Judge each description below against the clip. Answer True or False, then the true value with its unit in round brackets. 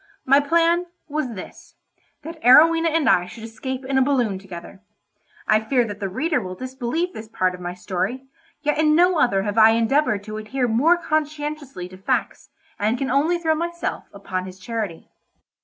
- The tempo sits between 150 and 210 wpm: True (175 wpm)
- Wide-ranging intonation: True (7.0 semitones)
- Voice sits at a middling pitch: False (250 Hz)